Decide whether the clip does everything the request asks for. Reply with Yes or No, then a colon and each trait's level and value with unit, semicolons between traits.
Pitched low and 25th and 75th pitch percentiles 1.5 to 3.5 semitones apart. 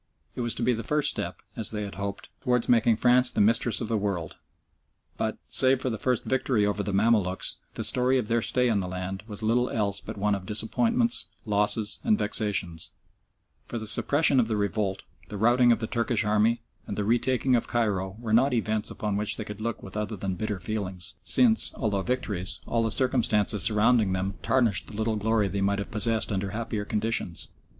Yes: low, 110 Hz; average, 2.8 semitones